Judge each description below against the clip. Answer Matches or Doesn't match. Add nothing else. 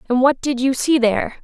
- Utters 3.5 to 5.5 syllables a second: Doesn't match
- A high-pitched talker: Matches